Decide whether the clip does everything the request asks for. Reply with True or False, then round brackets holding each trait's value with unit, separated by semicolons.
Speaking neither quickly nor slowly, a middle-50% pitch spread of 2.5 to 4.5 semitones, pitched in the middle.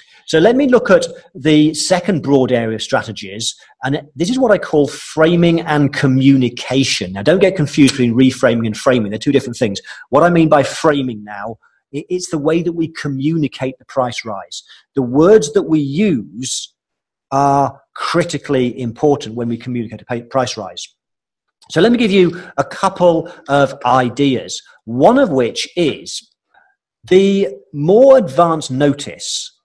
False (160 wpm; 5.2 semitones; 145 Hz)